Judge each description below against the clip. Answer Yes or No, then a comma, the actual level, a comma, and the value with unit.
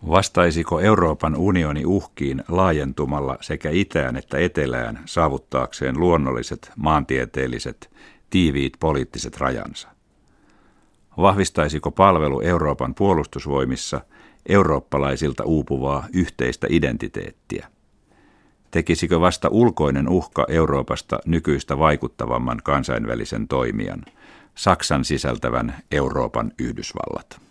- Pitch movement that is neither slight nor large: Yes, average, 4.1 semitones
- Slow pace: Yes, slow, 80 wpm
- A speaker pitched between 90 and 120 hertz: No, very low, 75 Hz